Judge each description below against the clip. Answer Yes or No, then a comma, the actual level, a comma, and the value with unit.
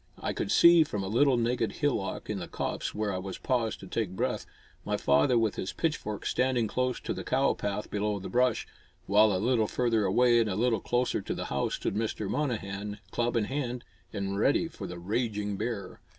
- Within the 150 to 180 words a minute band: No, fast, 205 wpm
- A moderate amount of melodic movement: Yes, average, 3.8 semitones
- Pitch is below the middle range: Yes, low, 110 Hz